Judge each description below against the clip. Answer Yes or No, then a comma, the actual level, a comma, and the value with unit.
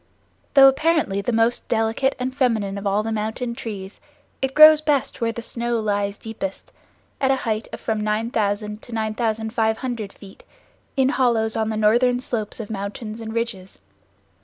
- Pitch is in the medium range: No, high, 225 Hz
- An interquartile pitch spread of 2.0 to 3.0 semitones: Yes, narrow, 2.6 semitones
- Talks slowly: No, average, 160 wpm